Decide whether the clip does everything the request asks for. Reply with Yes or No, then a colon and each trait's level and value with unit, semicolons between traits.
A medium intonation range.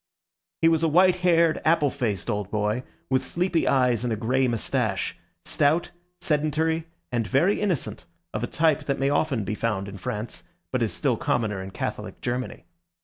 No: wide, 6.9 semitones